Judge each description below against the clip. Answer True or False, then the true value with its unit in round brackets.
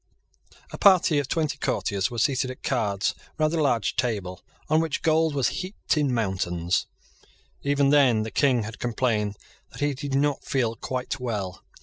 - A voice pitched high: False (130 Hz)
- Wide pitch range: False (5.0 semitones)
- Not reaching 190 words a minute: True (165 wpm)